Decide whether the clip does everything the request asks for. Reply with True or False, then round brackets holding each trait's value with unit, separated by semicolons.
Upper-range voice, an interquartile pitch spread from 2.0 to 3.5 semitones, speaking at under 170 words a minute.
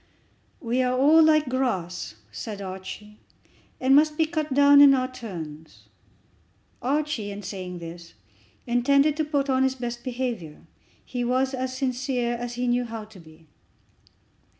False (245 Hz; 4.9 semitones; 150 wpm)